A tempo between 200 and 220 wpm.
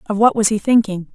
No: fast, 265 wpm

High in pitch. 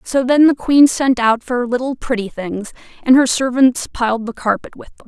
Yes: very high, 250 Hz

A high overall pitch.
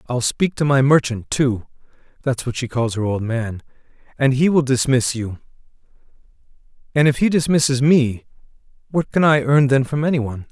No: low, 130 Hz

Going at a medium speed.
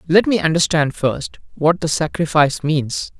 Yes: average, 150 wpm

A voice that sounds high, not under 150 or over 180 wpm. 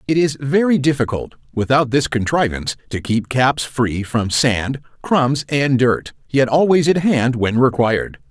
No: low, 130 Hz; average, 160 wpm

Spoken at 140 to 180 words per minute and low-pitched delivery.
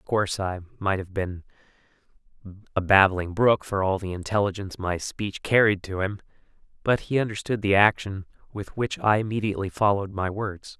Yes: average, 165 wpm; low, 100 Hz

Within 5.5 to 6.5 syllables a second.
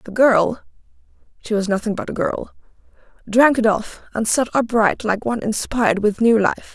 No: 5.0 syllables/s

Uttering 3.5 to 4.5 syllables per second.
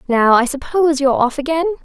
No: 6.2 syllables/s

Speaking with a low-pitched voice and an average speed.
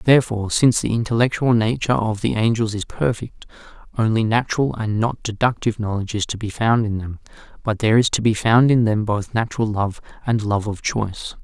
Yes: low, 110 Hz; average, 195 wpm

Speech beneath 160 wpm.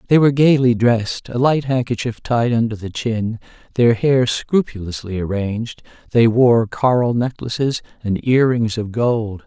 Yes: average, 150 wpm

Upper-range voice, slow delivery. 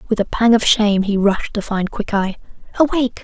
No: high, 215 Hz; fast, 205 wpm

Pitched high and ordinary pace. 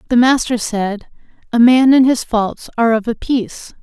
Yes: high, 235 Hz; average, 190 wpm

